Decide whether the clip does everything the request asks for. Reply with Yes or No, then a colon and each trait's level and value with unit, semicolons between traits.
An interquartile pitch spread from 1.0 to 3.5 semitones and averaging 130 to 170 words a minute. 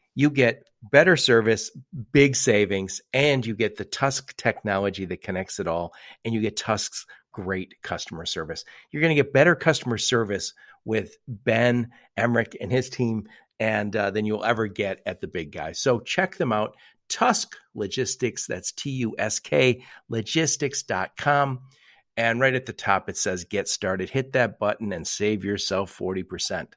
No: average, 4.4 semitones; average, 165 wpm